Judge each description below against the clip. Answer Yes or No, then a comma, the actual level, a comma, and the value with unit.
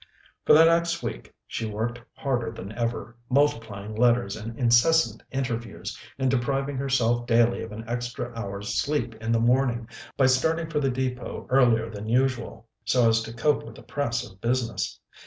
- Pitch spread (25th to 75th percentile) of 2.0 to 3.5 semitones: Yes, average, 2.8 semitones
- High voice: No, low, 120 Hz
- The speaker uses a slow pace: No, average, 170 wpm